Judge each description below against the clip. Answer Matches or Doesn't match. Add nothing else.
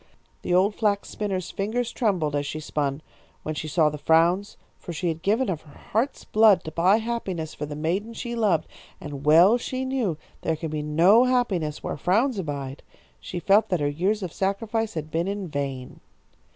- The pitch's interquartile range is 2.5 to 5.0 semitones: Doesn't match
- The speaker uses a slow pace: Doesn't match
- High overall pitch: Doesn't match